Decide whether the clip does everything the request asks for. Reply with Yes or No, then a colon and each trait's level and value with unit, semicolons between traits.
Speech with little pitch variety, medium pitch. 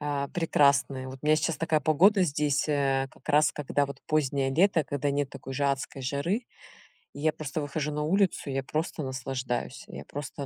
Yes: narrow, 2.1 semitones; medium, 145 Hz